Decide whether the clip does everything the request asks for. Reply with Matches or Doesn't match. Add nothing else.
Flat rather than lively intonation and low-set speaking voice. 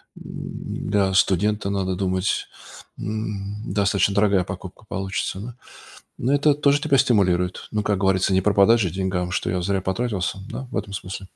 Matches